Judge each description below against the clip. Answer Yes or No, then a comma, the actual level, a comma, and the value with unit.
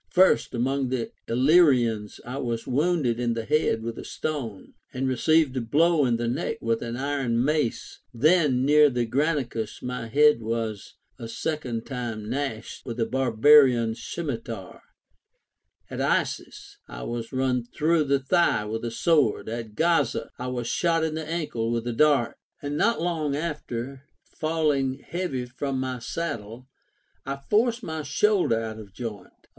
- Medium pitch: No, low, 130 Hz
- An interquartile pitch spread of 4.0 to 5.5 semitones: Yes, average, 4.6 semitones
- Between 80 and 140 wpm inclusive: No, average, 155 wpm